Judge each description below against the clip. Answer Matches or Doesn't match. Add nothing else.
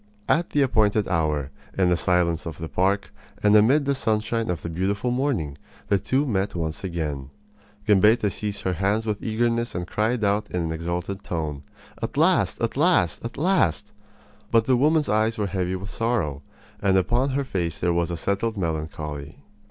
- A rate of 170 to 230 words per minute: Matches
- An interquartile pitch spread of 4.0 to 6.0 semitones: Matches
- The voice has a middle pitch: Doesn't match